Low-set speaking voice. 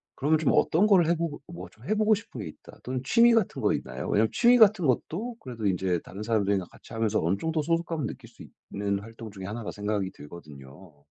Yes: low, 115 Hz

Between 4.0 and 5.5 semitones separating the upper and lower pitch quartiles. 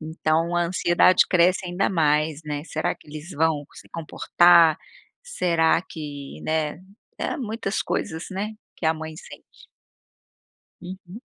No: narrow, 2.5 semitones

